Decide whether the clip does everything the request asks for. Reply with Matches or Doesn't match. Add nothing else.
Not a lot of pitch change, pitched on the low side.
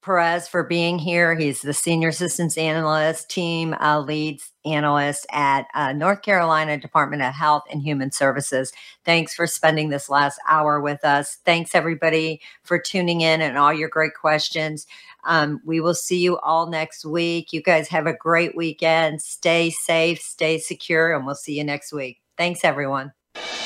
Doesn't match